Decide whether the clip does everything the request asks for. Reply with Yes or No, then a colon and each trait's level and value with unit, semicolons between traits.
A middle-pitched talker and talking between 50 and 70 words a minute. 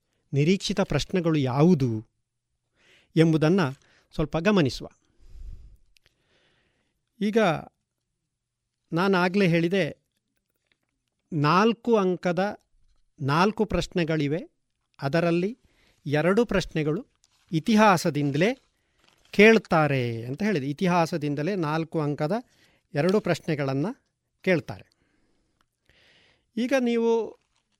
Yes: medium, 170 Hz; slow, 65 wpm